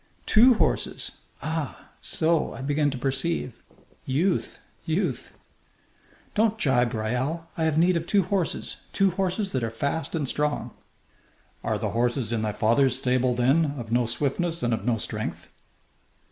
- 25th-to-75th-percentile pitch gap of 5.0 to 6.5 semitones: Yes, wide, 5.5 semitones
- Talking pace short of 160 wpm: Yes, average, 150 wpm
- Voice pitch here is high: No, medium, 145 Hz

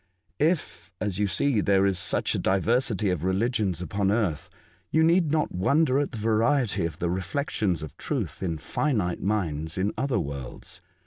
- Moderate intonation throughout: No, wide, 5.9 semitones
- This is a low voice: Yes, low, 100 Hz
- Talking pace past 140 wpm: Yes, average, 170 wpm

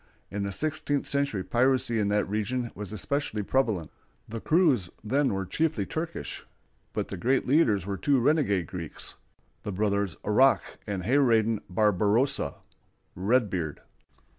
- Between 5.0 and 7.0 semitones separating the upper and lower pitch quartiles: Yes, average, 5.3 semitones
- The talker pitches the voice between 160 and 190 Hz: No, low, 110 Hz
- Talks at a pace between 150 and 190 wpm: No, slow, 135 wpm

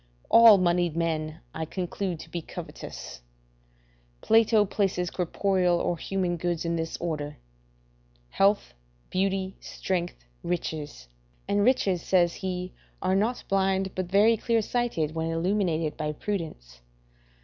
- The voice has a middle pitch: Yes, medium, 180 Hz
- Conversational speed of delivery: No, slow, 125 wpm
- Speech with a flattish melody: No, average, 3.2 semitones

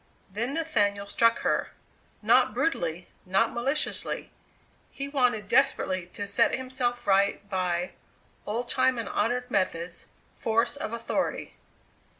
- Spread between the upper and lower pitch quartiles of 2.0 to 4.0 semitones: No, average, 4.7 semitones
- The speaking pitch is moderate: No, high, 230 Hz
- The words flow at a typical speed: No, slow, 120 wpm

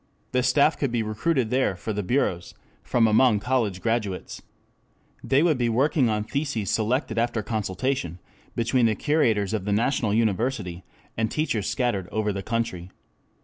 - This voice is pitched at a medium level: No, low, 115 Hz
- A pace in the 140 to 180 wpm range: Yes, average, 155 wpm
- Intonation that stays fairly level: No, average, 3.6 semitones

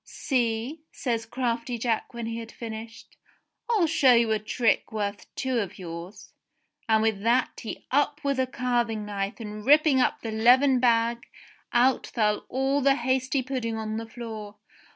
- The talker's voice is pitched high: Yes, high, 235 Hz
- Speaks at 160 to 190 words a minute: Yes, average, 165 wpm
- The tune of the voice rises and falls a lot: No, average, 2.8 semitones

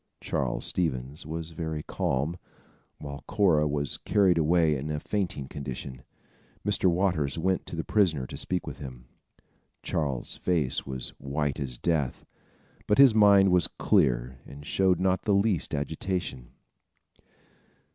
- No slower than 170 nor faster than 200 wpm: No, slow, 135 wpm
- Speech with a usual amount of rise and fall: Yes, average, 4.8 semitones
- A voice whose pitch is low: Yes, very low, 80 Hz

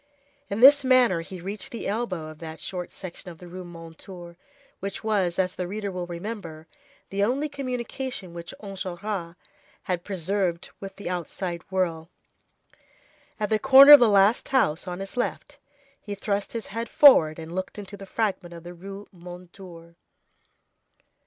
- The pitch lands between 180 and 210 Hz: Yes, high, 190 Hz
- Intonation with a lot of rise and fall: No, average, 3.6 semitones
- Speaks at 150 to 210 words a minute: Yes, average, 160 wpm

